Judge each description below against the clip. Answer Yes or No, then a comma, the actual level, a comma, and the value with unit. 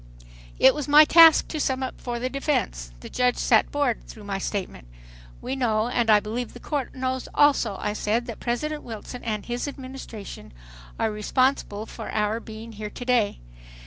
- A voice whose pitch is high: Yes, high, 240 Hz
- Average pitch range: Yes, average, 3.6 semitones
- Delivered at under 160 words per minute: No, average, 180 wpm